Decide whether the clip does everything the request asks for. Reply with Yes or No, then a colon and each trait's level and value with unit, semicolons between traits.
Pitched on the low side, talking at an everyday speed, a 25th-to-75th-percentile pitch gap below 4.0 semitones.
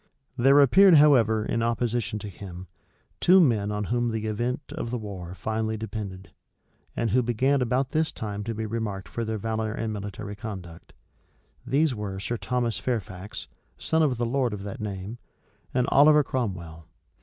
Yes: low, 110 Hz; average, 165 wpm; average, 3.5 semitones